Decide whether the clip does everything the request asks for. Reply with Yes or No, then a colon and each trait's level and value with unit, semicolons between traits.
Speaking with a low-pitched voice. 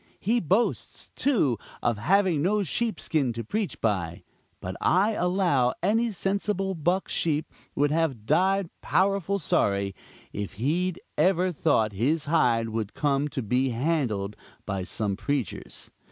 No: medium, 150 Hz